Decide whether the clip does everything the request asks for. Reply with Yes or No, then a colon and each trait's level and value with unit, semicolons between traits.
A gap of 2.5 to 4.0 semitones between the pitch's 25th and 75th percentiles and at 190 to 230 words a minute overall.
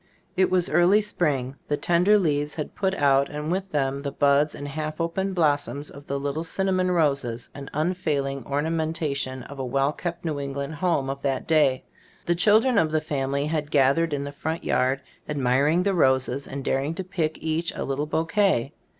Yes: average, 3.4 semitones; average, 195 wpm